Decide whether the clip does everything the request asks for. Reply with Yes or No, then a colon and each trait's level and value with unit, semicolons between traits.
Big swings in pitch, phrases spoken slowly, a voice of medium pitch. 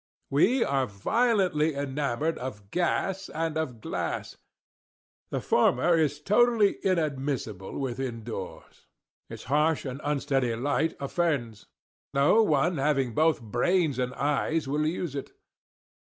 No: average, 4.1 semitones; slow, 120 wpm; medium, 145 Hz